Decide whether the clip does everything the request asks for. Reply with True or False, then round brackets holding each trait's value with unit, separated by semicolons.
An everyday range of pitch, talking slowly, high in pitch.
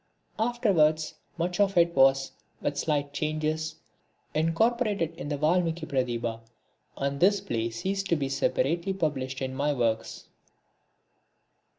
False (4.4 semitones; 120 wpm; 155 Hz)